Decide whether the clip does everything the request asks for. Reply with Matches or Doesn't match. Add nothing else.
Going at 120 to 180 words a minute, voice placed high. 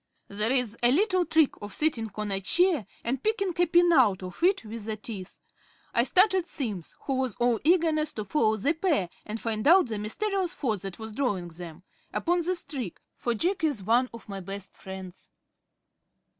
Doesn't match